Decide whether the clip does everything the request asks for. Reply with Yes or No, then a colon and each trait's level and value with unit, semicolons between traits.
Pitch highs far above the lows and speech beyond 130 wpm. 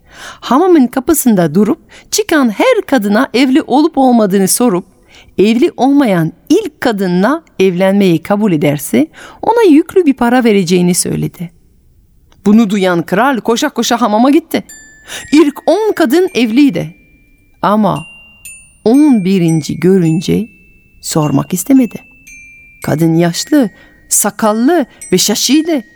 No: wide, 7.6 semitones; average, 105 wpm